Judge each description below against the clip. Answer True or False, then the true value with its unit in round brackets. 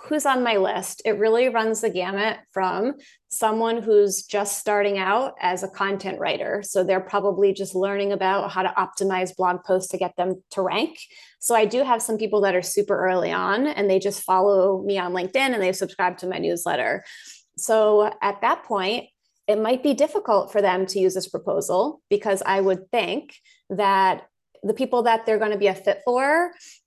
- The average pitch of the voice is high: True (200 Hz)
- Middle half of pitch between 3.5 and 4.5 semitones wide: False (3.0 semitones)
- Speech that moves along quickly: False (195 wpm)